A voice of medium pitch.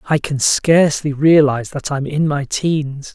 Yes: medium, 145 Hz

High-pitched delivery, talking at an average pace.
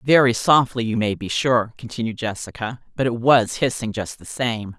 No: low, 120 Hz; average, 190 wpm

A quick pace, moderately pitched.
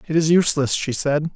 Yes: fast, 220 wpm; medium, 155 Hz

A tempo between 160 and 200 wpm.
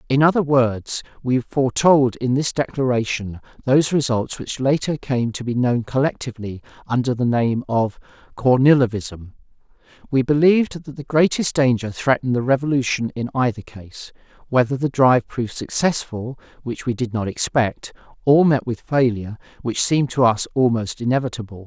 No: average, 145 wpm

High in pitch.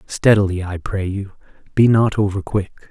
No: low, 100 Hz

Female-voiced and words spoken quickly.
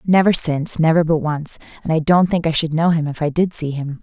Yes: female; fast, 270 wpm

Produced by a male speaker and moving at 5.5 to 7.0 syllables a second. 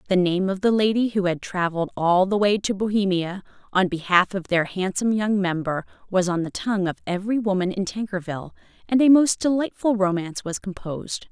No: female; 5.8 syllables/s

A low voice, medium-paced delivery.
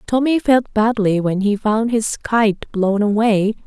No: high, 215 Hz; average, 165 wpm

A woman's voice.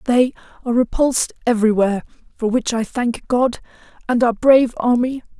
Yes: female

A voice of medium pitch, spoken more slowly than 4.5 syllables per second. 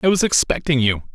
No: medium, 145 Hz; 5.8 syllables/s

